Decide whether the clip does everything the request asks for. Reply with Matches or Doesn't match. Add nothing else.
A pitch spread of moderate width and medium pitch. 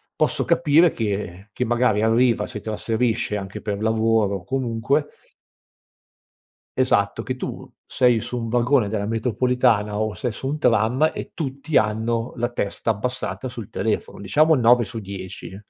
Doesn't match